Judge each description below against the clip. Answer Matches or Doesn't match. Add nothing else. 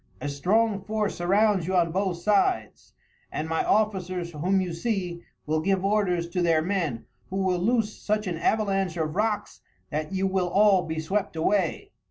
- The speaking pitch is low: Doesn't match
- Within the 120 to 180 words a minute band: Matches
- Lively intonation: Doesn't match